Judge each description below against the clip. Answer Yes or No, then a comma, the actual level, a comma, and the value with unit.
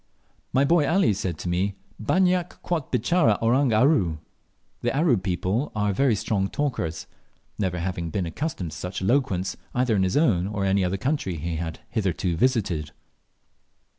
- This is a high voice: No, low, 100 Hz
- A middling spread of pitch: No, wide, 7.0 semitones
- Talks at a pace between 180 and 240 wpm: No, average, 160 wpm